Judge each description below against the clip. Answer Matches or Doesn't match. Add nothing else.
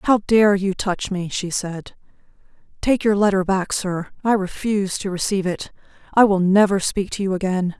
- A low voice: Doesn't match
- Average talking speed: Matches